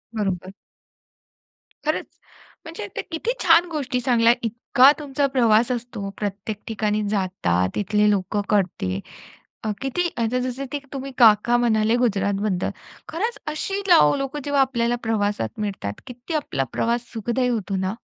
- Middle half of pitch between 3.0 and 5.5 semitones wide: Yes, average, 4.3 semitones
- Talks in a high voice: Yes, high, 230 Hz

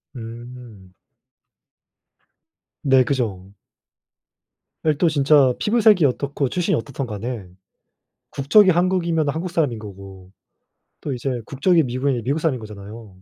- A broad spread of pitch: Yes, wide, 5.8 semitones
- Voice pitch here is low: Yes, low, 130 Hz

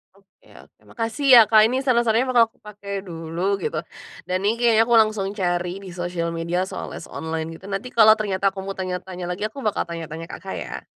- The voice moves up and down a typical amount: Yes, average, 3.9 semitones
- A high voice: Yes, high, 195 Hz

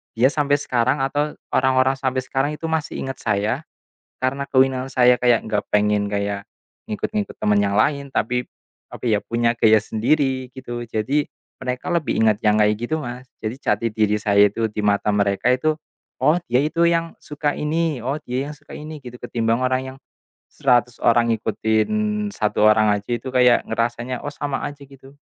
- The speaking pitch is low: Yes, low, 125 Hz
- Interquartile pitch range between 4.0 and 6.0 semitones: Yes, average, 4.3 semitones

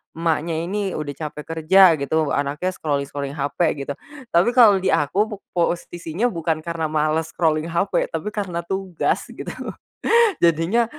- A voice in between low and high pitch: Yes, medium, 165 Hz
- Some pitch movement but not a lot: Yes, average, 3.6 semitones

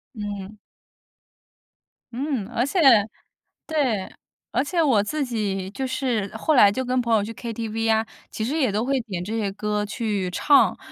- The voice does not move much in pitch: No, average, 4.0 semitones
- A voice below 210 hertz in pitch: No, high, 225 Hz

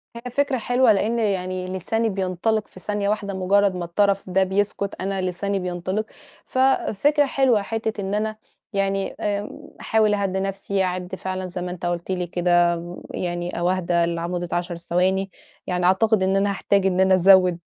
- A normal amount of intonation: No, narrow, 2.3 semitones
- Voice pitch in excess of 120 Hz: Yes, high, 190 Hz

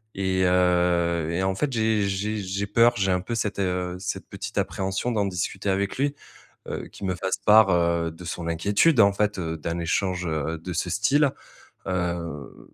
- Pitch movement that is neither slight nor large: Yes, average, 3.0 semitones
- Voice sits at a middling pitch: No, very low, 95 Hz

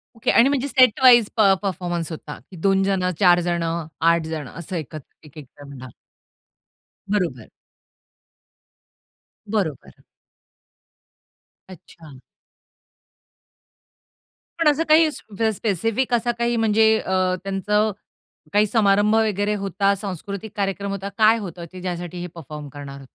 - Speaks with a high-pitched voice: Yes, high, 195 Hz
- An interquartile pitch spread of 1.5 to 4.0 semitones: No, average, 4.5 semitones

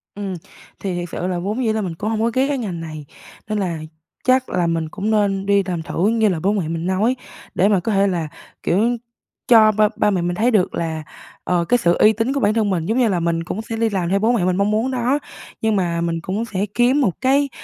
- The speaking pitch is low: No, high, 200 Hz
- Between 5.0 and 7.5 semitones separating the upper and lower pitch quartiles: No, average, 4.3 semitones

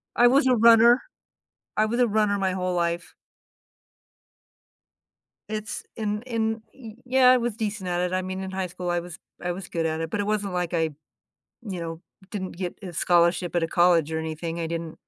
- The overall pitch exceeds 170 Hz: Yes, medium, 185 Hz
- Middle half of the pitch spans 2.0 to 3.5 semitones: No, average, 3.9 semitones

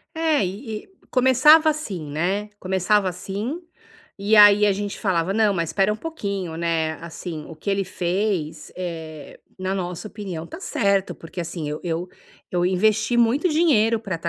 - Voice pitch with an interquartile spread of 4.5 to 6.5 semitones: No, average, 4.1 semitones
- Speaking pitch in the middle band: No, high, 195 Hz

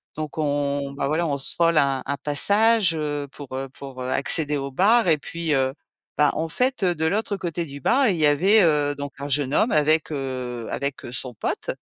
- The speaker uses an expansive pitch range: No, average, 3.3 semitones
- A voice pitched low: No, medium, 145 Hz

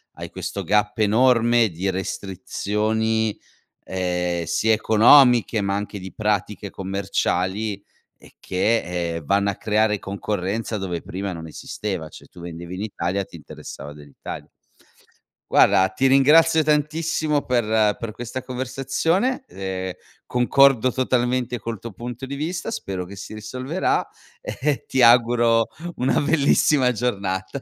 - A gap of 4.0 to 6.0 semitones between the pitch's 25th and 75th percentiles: Yes, average, 4.8 semitones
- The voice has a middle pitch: No, low, 110 Hz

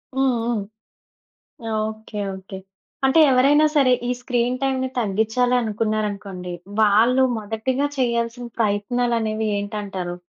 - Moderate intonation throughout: Yes, average, 3.3 semitones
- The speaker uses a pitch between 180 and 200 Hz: No, high, 225 Hz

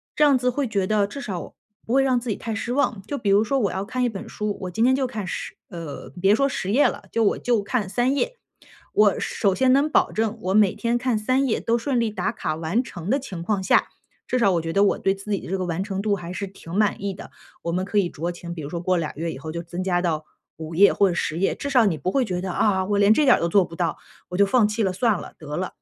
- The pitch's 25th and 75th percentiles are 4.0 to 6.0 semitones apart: Yes, average, 4.8 semitones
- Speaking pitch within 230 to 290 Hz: No, high, 200 Hz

